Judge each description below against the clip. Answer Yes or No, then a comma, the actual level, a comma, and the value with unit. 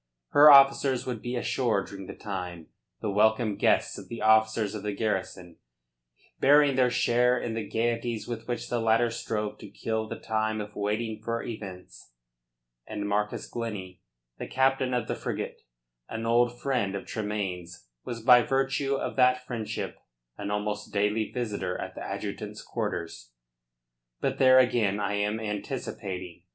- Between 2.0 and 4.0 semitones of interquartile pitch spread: Yes, average, 2.9 semitones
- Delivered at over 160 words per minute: No, average, 155 wpm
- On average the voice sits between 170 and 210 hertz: No, low, 110 Hz